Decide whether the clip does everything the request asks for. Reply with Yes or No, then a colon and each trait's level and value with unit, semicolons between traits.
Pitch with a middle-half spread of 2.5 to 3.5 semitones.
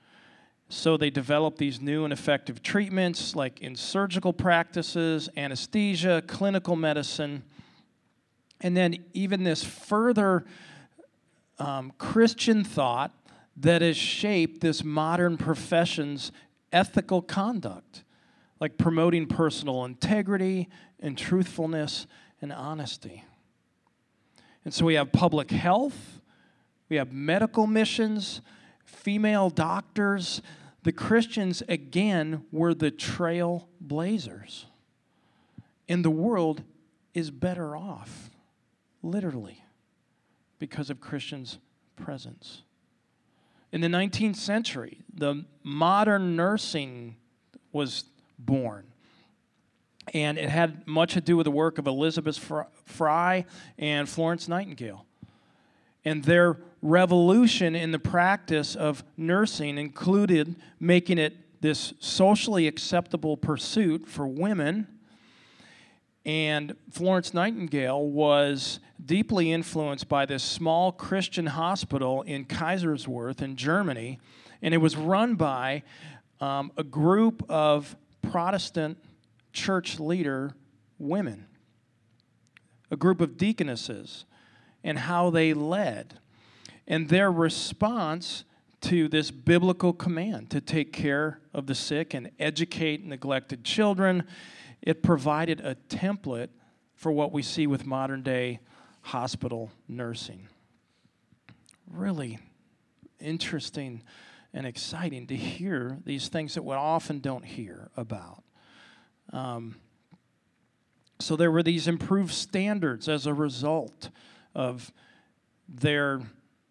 No: average, 4.0 semitones